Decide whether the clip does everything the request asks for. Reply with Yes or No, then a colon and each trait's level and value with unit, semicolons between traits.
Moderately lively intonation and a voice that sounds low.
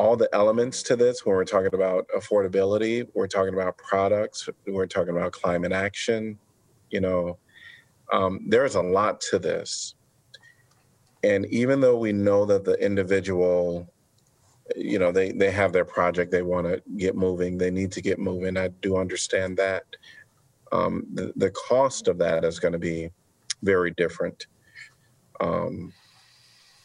No: wide, 6.6 semitones; low, 100 Hz